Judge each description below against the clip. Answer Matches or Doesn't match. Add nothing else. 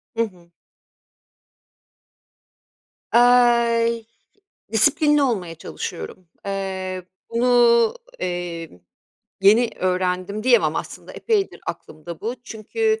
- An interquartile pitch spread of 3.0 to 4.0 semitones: Doesn't match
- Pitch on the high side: Matches